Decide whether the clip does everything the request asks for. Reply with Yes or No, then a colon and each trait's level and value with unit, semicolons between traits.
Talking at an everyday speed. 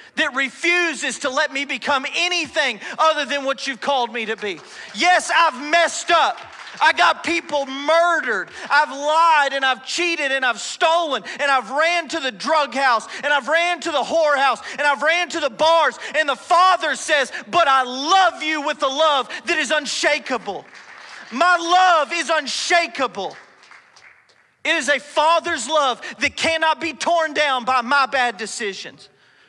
Yes: average, 165 wpm